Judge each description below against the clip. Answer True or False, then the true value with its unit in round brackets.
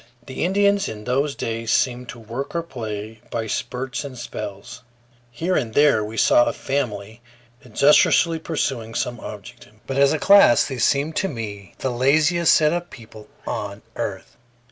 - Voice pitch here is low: True (130 Hz)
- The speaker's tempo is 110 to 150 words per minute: False (165 wpm)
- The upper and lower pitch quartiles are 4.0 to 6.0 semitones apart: True (5.1 semitones)